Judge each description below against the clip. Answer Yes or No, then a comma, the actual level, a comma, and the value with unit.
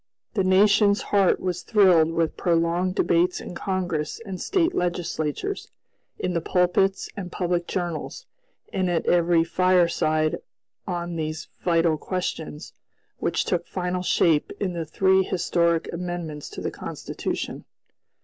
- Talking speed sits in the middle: No, slow, 130 wpm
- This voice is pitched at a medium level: Yes, medium, 175 Hz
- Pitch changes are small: Yes, narrow, 2.0 semitones